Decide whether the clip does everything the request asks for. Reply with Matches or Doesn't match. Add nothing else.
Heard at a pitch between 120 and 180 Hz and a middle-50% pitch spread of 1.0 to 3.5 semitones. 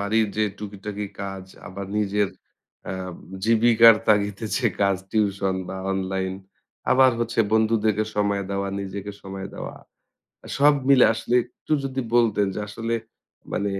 Doesn't match